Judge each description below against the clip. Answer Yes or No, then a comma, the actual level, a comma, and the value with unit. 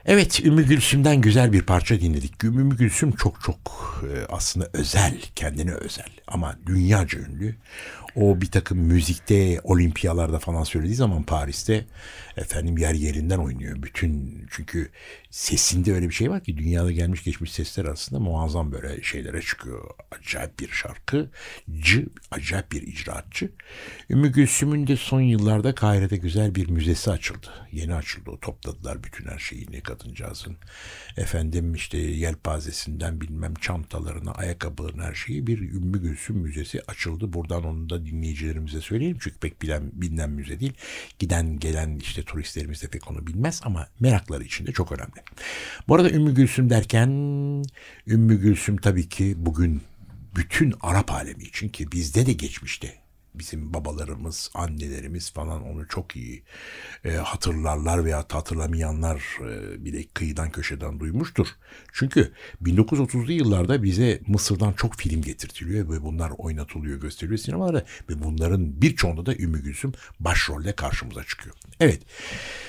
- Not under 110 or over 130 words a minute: No, fast, 140 wpm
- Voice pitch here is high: No, very low, 85 Hz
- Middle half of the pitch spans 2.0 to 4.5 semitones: No, average, 5.1 semitones